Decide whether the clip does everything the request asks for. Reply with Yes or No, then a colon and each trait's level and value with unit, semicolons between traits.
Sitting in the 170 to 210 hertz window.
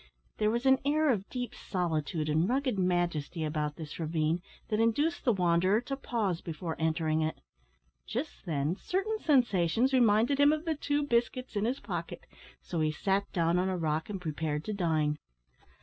Yes: medium, 185 Hz